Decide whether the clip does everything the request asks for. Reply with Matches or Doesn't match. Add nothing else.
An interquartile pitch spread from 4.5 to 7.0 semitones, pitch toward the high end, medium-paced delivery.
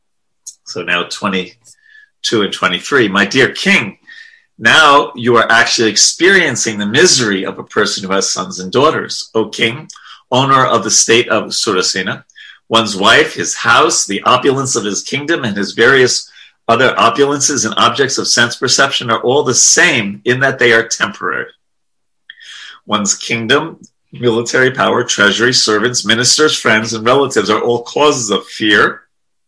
Doesn't match